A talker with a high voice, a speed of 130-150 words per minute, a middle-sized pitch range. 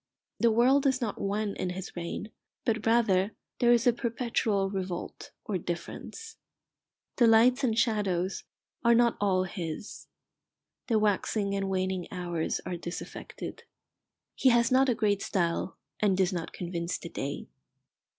Yes: high, 205 Hz; average, 145 wpm; average, 4.2 semitones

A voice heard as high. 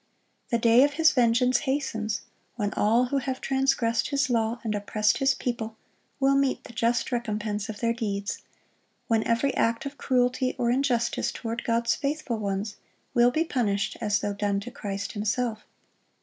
Yes: high, 235 Hz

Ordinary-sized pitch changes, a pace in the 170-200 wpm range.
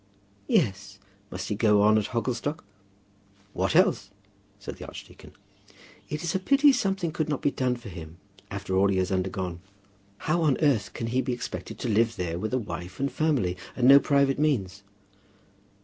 No: wide, 7.1 semitones; average, 180 wpm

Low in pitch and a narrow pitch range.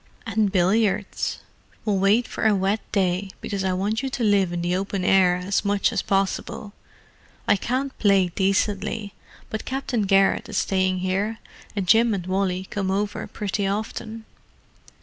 No: high, 200 Hz; narrow, 2.1 semitones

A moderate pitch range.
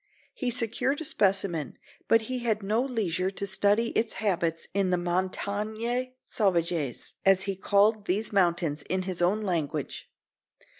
Yes: average, 3.5 semitones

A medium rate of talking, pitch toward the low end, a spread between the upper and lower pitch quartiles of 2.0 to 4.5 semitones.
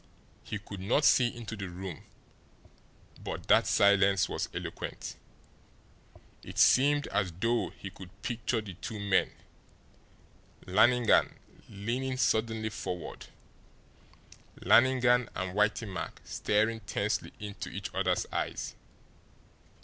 No: slow, 110 wpm; low, 105 Hz; average, 3.5 semitones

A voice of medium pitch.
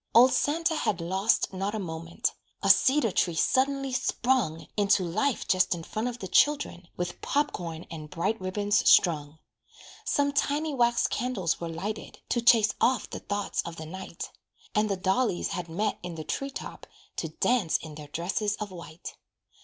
No: high, 195 Hz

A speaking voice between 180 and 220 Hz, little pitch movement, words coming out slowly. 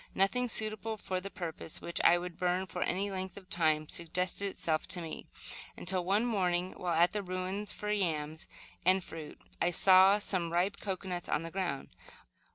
No: medium, 185 Hz; narrow, 2.3 semitones; average, 170 wpm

